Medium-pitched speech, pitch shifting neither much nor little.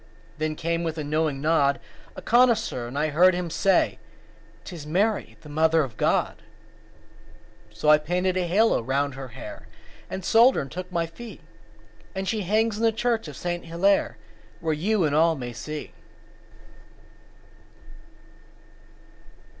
Yes: medium, 165 Hz; average, 4.3 semitones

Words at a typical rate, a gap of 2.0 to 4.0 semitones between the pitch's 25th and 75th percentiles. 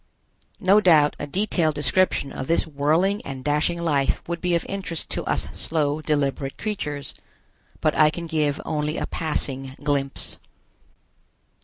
Yes: average, 145 wpm; average, 3.0 semitones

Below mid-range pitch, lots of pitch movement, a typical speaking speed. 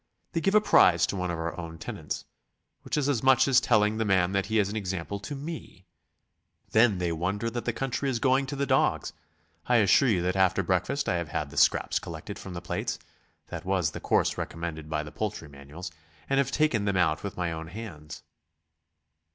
No: low, 100 Hz; wide, 6.1 semitones; fast, 215 wpm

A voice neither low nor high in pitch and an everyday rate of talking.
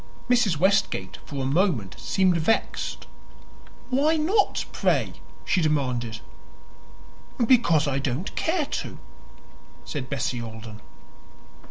No: medium, 155 Hz; slow, 105 wpm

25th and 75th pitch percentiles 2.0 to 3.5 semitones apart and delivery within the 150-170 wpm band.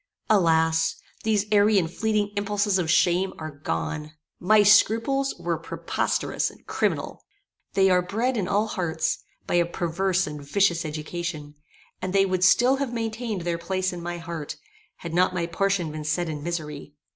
No: average, 4.0 semitones; average, 165 wpm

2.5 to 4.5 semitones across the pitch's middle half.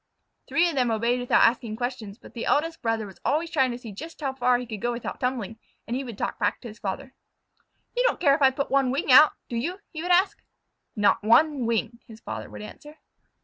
Yes: average, 4.1 semitones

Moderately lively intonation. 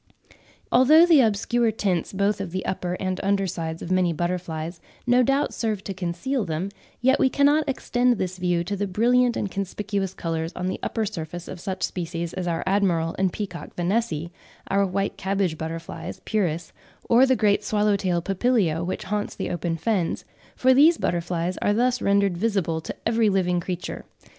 Yes: average, 4.0 semitones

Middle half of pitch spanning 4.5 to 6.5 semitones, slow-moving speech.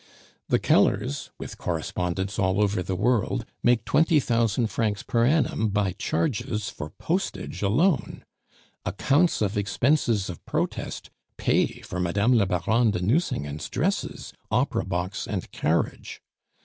Yes: average, 4.9 semitones; slow, 130 wpm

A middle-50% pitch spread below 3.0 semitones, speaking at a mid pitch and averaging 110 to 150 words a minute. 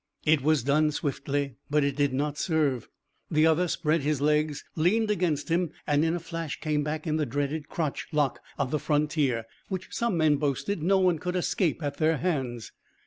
No: narrow, 2.4 semitones; medium, 150 Hz; average, 195 wpm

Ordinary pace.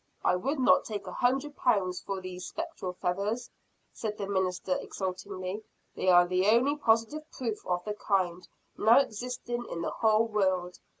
Yes: average, 165 wpm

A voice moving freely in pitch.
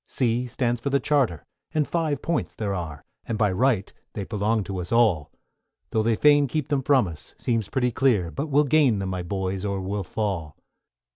Yes: wide, 5.9 semitones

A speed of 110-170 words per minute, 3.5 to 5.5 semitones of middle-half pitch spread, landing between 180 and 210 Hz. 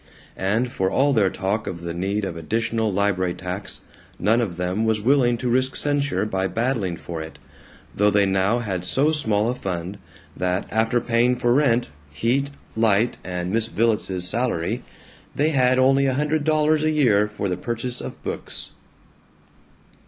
No: average, 165 wpm; average, 4.9 semitones; low, 110 Hz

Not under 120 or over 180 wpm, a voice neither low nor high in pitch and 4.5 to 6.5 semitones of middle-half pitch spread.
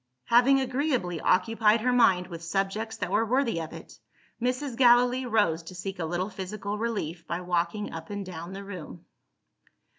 No: average, 170 wpm; high, 200 Hz; average, 5.1 semitones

